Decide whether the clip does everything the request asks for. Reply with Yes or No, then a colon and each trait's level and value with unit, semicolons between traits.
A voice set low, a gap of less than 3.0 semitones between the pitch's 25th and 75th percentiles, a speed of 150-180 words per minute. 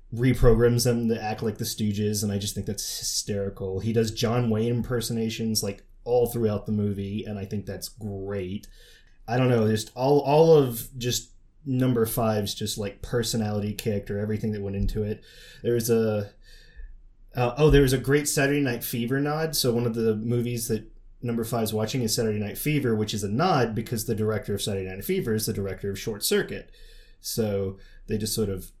No: low, 110 Hz; narrow, 2.6 semitones; average, 200 wpm